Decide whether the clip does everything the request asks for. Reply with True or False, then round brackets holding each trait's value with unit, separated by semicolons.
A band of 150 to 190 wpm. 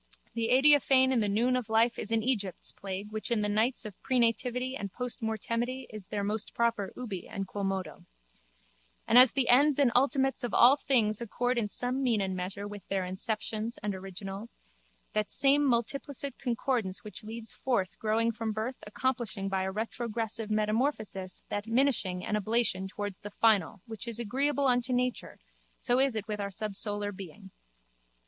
True (170 wpm)